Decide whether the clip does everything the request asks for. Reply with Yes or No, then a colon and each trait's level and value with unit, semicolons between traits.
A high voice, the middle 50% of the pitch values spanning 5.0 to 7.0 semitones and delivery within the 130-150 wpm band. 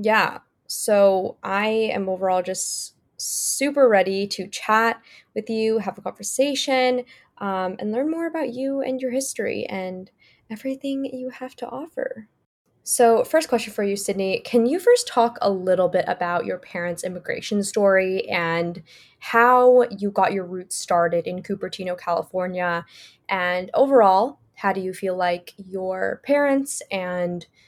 Yes: high, 200 Hz; wide, 5.4 semitones; average, 145 wpm